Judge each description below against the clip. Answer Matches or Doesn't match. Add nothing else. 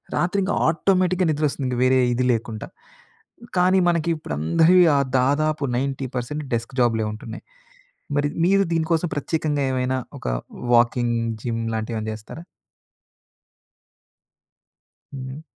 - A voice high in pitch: Doesn't match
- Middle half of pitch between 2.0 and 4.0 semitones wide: Doesn't match